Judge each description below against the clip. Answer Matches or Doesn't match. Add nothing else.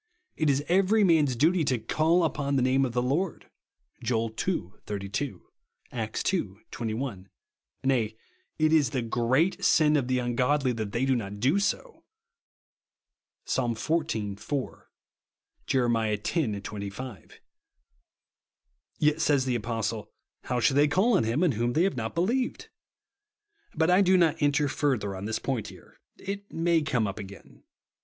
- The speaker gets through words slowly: Doesn't match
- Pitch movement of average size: Doesn't match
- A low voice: Matches